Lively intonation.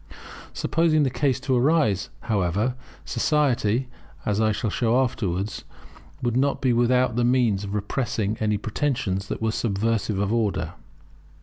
No: average, 3.9 semitones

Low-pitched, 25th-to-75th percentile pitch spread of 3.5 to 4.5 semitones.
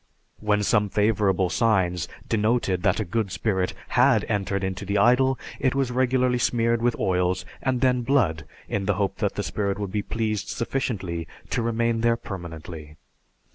Yes: low, 105 Hz; average, 3.9 semitones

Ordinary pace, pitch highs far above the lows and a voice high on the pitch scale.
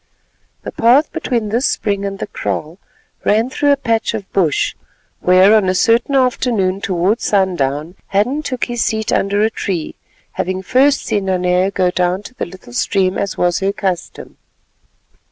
No: average, 165 wpm; average, 3.9 semitones; high, 200 Hz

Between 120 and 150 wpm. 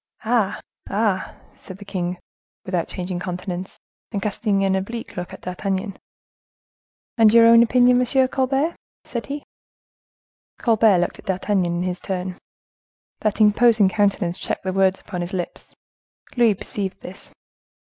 Yes: average, 140 wpm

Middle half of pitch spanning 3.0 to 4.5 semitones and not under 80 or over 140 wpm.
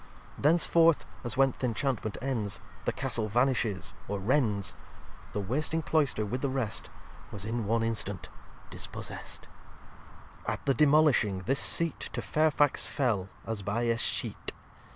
No: average, 4.9 semitones; slow, 135 wpm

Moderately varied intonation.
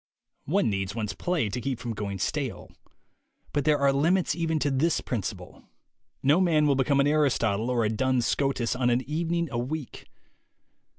Yes: average, 4.5 semitones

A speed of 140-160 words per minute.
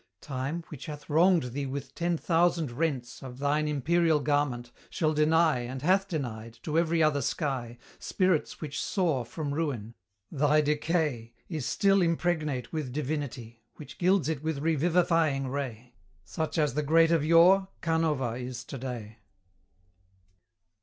Yes: average, 145 wpm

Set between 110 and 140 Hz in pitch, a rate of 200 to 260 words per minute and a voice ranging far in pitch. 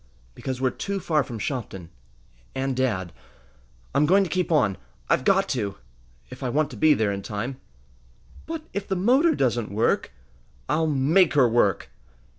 No: low, 135 Hz; average, 165 wpm; wide, 7.4 semitones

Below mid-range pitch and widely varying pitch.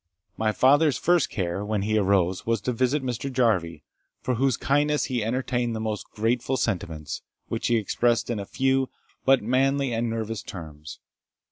No: low, 115 Hz; average, 4.2 semitones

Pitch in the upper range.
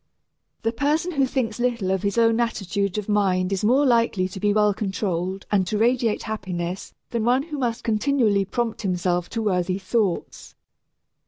Yes: high, 210 Hz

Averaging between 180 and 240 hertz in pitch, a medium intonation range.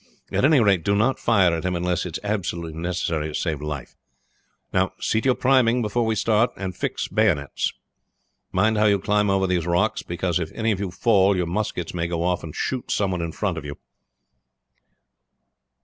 No: very low, 95 Hz; average, 3.9 semitones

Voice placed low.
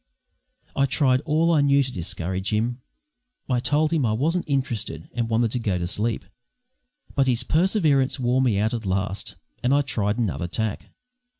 Yes: low, 120 Hz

